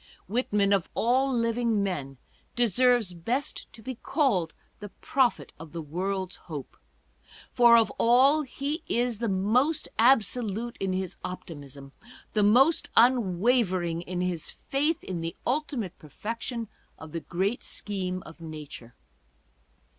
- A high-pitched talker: Yes, high, 210 Hz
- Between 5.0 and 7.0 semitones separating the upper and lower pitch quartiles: Yes, wide, 5.6 semitones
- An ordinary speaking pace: No, slow, 130 wpm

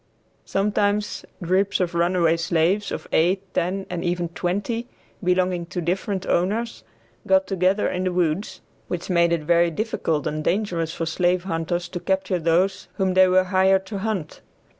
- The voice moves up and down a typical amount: No, narrow, 2.2 semitones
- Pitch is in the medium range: Yes, medium, 180 Hz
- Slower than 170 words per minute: Yes, average, 160 wpm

